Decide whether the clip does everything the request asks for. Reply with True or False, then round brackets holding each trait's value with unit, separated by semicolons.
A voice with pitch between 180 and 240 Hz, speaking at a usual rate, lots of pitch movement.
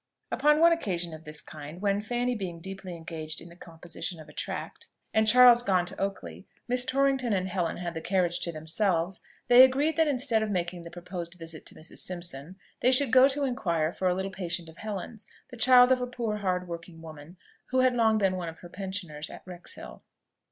False (185 Hz; 210 wpm; 6.2 semitones)